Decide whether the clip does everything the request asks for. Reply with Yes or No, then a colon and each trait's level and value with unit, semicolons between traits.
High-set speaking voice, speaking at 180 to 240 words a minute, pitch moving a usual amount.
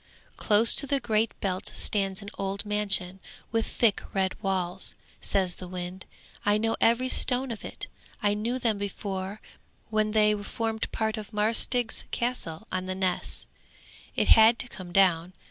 No: high, 210 Hz; average, 165 wpm; average, 3.0 semitones